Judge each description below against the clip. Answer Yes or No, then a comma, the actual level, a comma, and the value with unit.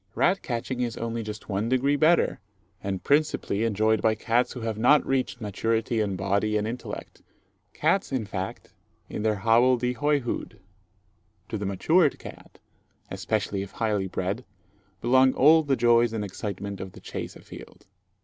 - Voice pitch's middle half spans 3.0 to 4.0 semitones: Yes, average, 3.7 semitones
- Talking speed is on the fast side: No, average, 165 wpm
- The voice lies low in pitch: Yes, low, 115 Hz